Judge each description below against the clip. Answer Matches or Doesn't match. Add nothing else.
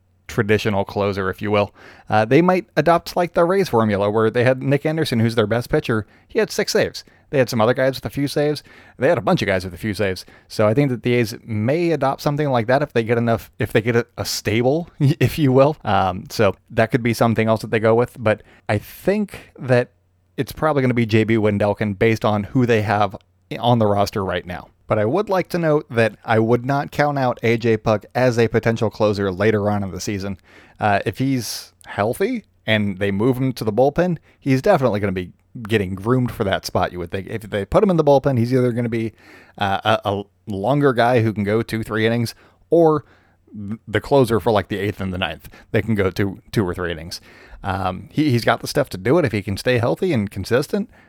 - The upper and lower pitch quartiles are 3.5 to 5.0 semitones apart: Matches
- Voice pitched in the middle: Doesn't match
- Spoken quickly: Matches